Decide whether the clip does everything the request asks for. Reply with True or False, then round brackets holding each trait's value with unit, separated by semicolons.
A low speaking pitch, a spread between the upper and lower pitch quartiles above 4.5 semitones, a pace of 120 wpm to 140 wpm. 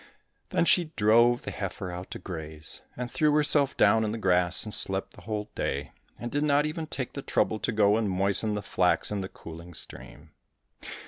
False (105 Hz; 5.0 semitones; 200 wpm)